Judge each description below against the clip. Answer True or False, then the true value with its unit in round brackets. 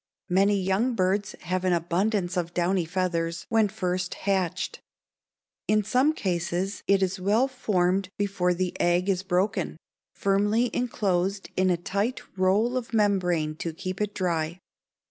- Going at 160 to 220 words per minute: False (145 wpm)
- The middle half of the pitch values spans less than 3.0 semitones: True (2.5 semitones)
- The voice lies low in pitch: False (190 Hz)